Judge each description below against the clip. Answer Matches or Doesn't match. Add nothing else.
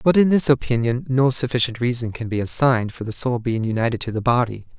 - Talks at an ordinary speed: Doesn't match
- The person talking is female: Doesn't match